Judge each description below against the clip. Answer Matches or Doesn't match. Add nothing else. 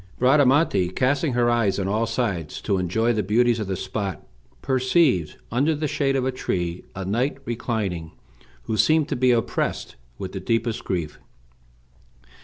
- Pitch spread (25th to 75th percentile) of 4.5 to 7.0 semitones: Matches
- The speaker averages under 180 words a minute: Matches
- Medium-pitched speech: Doesn't match